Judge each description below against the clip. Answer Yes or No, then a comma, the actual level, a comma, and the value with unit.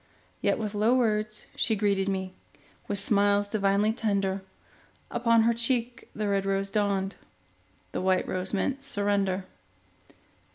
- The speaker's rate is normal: No, slow, 130 wpm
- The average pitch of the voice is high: Yes, high, 205 Hz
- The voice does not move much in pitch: Yes, narrow, 2.1 semitones